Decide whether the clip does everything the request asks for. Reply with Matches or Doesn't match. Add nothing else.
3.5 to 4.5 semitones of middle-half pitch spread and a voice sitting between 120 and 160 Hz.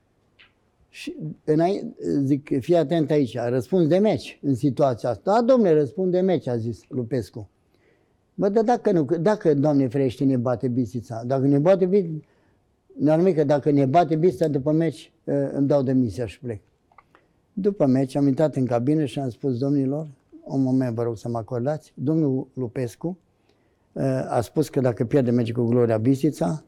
Matches